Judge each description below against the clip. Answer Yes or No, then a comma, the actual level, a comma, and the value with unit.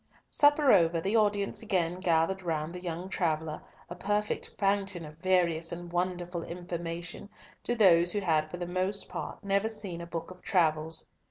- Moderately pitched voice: Yes, medium, 175 Hz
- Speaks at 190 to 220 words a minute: No, average, 170 wpm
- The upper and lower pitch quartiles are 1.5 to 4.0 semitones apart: Yes, average, 2.8 semitones